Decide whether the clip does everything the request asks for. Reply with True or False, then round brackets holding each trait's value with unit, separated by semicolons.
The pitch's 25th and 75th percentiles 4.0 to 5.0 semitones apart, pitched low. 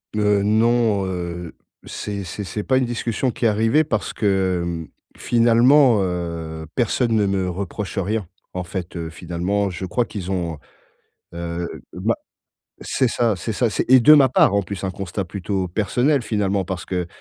True (4.3 semitones; 100 Hz)